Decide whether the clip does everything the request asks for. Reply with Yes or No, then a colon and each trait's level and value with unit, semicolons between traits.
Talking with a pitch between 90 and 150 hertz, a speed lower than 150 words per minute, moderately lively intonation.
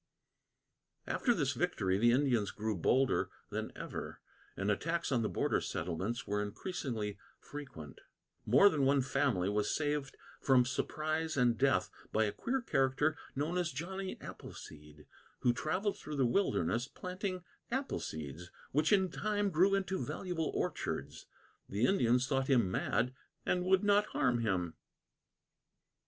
No: low, 135 Hz; average, 140 wpm; wide, 8.5 semitones